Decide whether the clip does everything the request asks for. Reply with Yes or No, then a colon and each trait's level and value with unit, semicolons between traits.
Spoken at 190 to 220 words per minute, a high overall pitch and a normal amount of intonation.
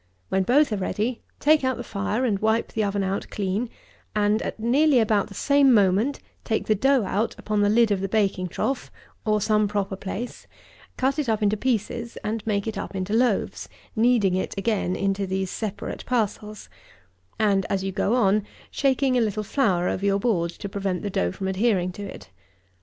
Yes: average, 195 wpm; high, 210 Hz; average, 3.2 semitones